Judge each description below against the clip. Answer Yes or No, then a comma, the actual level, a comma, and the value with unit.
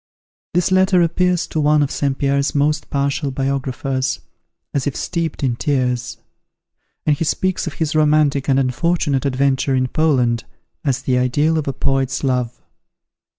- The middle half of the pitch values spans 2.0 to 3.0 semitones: Yes, average, 2.7 semitones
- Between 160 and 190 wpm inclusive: No, average, 150 wpm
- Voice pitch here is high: No, medium, 140 Hz